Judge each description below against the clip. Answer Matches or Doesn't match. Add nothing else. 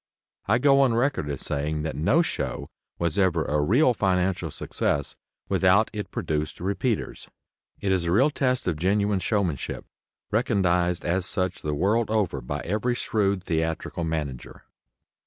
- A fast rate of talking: Doesn't match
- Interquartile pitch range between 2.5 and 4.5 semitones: Doesn't match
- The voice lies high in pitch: Doesn't match